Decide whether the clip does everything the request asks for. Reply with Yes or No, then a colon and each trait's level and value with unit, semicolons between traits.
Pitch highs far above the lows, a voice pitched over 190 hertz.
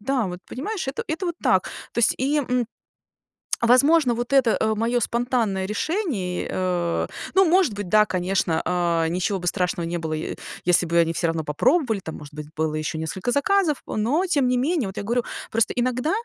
Yes: wide, 7.1 semitones; high, 225 Hz